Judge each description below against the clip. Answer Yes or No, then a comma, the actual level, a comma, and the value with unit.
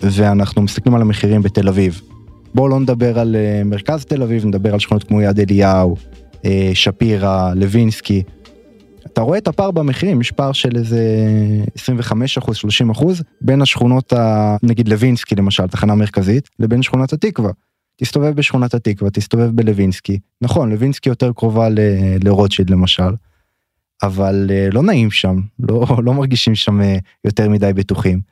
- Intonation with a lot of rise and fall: No, average, 3.6 semitones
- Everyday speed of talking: Yes, average, 140 wpm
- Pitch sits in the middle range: No, low, 110 Hz